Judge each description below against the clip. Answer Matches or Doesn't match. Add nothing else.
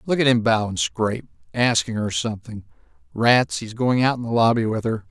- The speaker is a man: Matches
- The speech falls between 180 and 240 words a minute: Matches